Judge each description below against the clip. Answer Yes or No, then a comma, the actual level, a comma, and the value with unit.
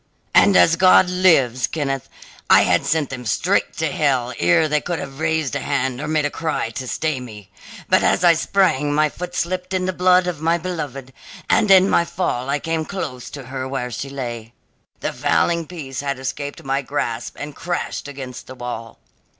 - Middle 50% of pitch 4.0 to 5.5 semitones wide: Yes, average, 4.5 semitones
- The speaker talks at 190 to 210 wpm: Yes, average, 195 wpm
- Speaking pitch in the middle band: Yes, medium, 145 Hz